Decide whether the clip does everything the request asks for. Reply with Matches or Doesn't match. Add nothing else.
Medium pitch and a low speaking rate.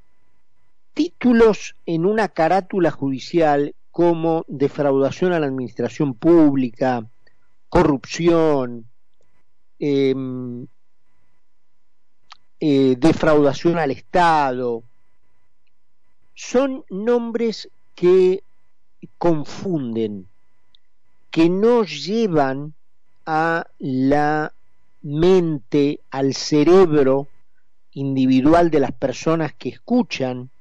Matches